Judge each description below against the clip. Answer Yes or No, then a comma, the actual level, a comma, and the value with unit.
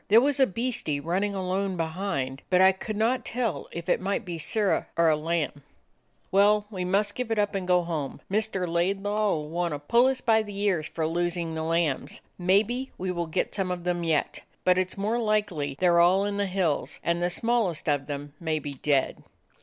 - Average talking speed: No, fast, 215 wpm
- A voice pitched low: No, medium, 180 Hz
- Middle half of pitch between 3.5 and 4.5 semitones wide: Yes, average, 3.9 semitones